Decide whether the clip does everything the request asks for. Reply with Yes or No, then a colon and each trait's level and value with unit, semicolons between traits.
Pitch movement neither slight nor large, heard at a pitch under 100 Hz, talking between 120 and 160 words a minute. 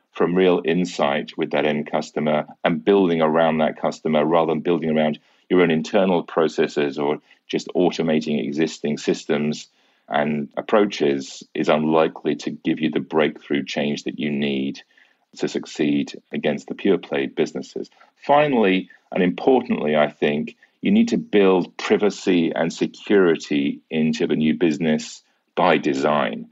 Yes: average, 3.1 semitones; very low, 80 Hz; average, 145 wpm